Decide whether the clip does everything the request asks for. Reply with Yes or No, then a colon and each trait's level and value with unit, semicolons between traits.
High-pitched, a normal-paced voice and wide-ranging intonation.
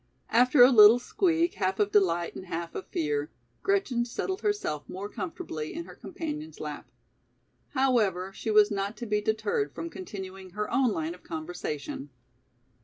Yes: high, 205 Hz; average, 160 wpm; wide, 5.9 semitones